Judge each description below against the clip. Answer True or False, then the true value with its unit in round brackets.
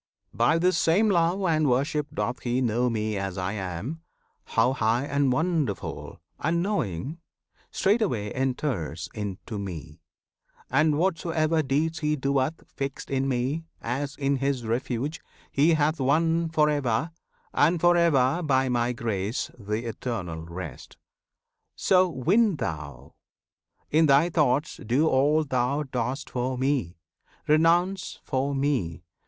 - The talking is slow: True (130 wpm)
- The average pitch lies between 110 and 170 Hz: True (135 Hz)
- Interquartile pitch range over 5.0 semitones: True (5.4 semitones)